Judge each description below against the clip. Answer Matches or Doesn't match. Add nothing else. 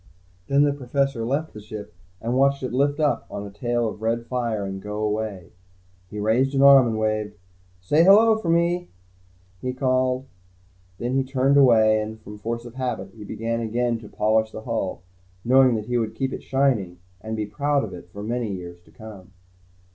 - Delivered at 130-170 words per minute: Doesn't match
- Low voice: Matches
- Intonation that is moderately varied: Matches